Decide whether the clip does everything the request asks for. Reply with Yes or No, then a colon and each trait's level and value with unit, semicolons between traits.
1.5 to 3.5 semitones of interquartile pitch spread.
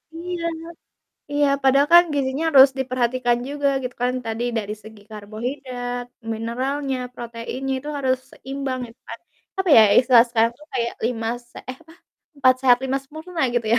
Yes: average, 2.8 semitones